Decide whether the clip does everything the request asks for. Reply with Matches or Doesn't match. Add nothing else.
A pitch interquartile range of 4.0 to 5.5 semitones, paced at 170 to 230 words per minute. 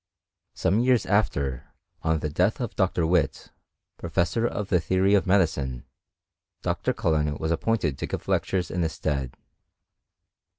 Doesn't match